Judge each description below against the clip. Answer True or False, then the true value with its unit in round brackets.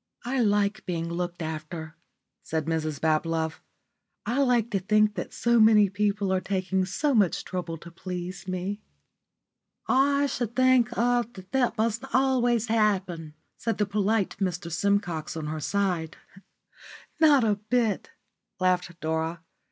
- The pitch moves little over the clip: False (5.1 semitones)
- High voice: True (195 Hz)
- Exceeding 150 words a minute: False (145 wpm)